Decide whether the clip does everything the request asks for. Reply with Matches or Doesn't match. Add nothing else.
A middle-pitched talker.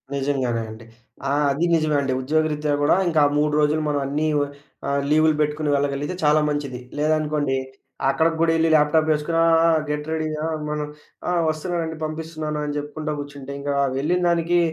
Matches